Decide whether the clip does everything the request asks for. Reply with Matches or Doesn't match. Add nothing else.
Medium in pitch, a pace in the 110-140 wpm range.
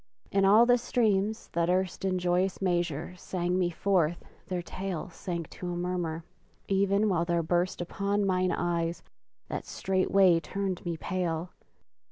Doesn't match